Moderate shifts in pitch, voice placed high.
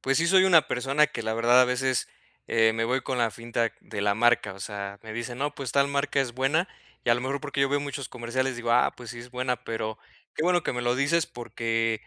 No: average, 3.2 semitones; low, 125 Hz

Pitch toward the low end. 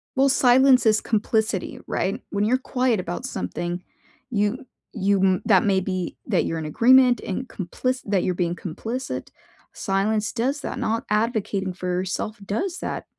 No: high, 210 Hz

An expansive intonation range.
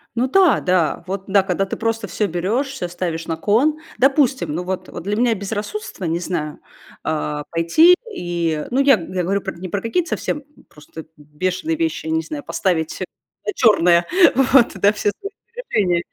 Yes: wide, 7.4 semitones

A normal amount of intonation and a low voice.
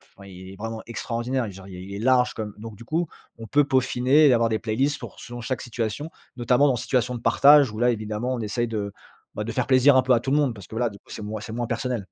Yes: average, 3.1 semitones; low, 120 Hz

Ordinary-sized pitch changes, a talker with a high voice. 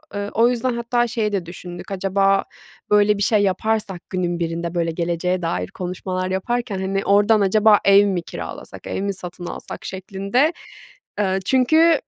Yes: average, 3.0 semitones; high, 195 Hz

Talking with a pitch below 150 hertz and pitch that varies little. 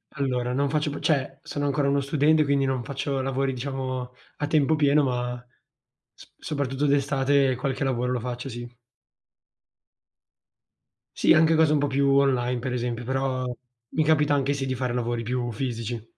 Yes: low, 135 Hz; narrow, 2.3 semitones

